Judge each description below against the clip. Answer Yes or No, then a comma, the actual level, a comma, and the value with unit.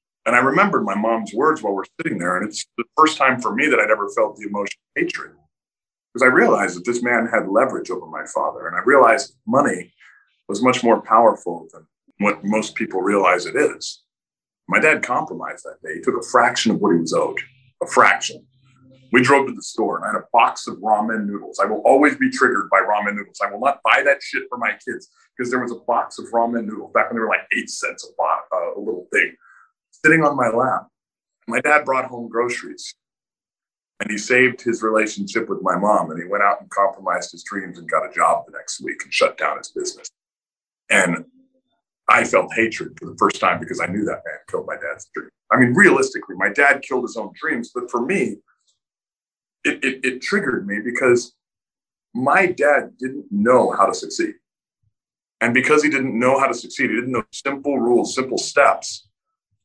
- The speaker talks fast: Yes, fast, 210 wpm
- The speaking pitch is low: Yes, low, 130 Hz